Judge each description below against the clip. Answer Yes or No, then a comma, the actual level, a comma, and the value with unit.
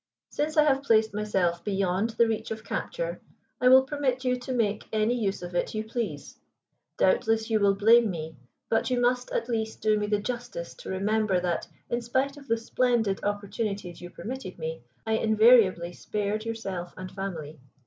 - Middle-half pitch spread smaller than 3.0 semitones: No, average, 3.8 semitones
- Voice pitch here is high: Yes, high, 220 Hz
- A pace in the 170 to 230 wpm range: Yes, average, 180 wpm